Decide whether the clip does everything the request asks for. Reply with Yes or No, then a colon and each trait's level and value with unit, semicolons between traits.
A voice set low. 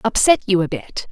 No: high, 200 Hz